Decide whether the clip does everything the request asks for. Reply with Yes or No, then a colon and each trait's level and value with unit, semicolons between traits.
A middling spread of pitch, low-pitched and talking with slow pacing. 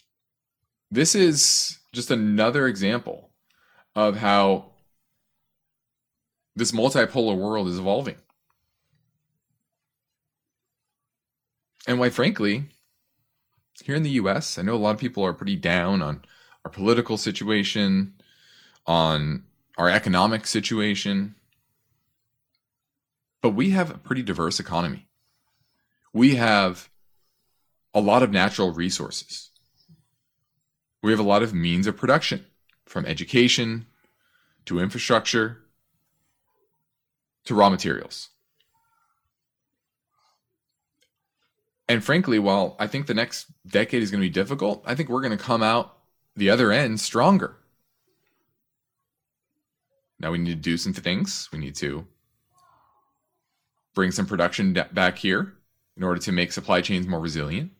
No: wide, 6.7 semitones; low, 115 Hz; slow, 115 wpm